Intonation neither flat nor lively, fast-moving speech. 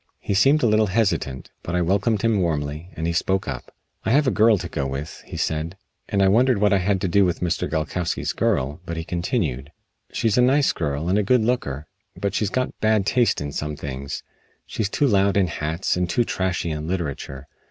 No: wide, 5.7 semitones; fast, 215 wpm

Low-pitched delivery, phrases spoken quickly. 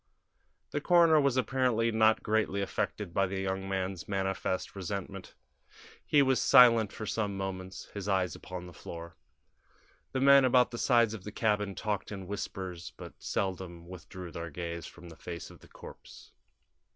No: low, 100 Hz; average, 165 wpm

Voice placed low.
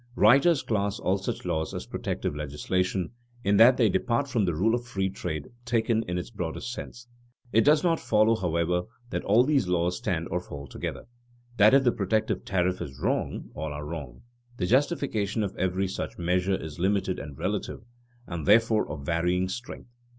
Yes: very low, 95 Hz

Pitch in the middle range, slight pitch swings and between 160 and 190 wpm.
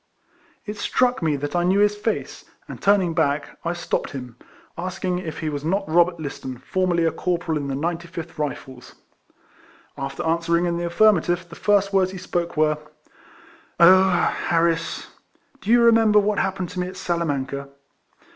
No: medium, 175 Hz; average, 3.3 semitones; average, 175 wpm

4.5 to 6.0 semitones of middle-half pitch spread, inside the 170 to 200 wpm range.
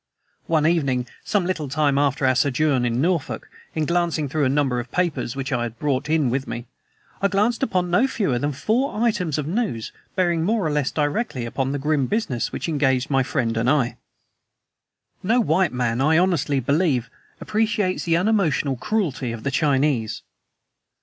Yes: average, 5.3 semitones; average, 175 wpm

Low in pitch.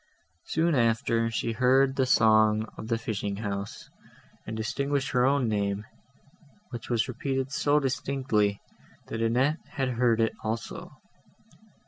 Yes: low, 115 Hz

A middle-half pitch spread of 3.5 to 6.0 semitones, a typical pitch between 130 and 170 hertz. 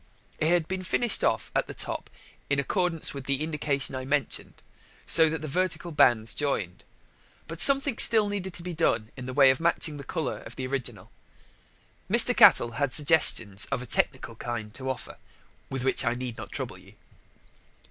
Yes: average, 4.7 semitones; medium, 140 Hz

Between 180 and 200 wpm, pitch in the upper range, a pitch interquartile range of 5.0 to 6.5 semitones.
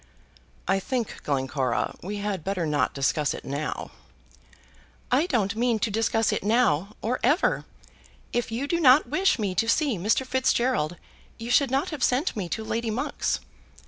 No: average, 165 wpm; high, 225 Hz; wide, 5.4 semitones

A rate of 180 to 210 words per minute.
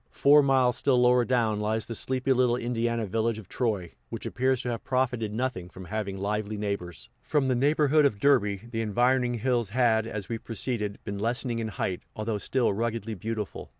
Yes: average, 185 wpm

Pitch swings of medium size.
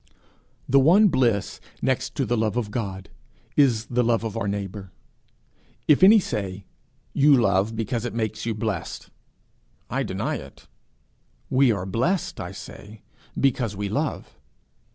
Yes: average, 4.0 semitones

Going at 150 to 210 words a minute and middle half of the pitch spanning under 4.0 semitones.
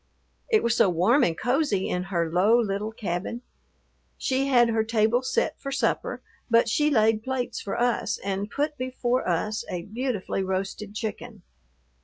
No: average, 160 wpm; average, 4.3 semitones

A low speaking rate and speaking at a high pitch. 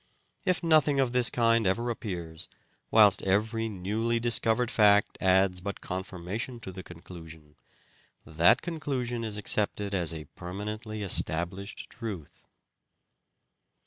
No: slow, 125 wpm; low, 105 Hz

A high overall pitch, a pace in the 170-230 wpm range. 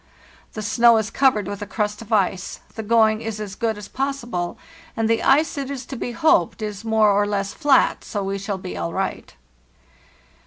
Yes: high, 215 Hz; average, 200 wpm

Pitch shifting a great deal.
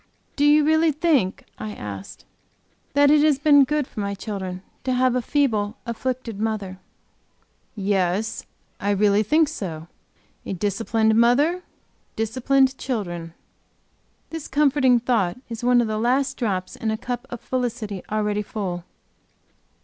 No: average, 4.9 semitones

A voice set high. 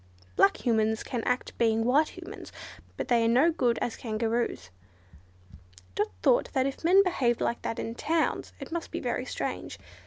Yes: high, 240 Hz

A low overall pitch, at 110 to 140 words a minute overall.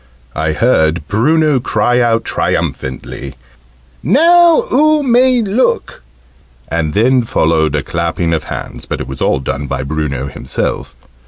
Yes: very low, 90 Hz; slow, 135 wpm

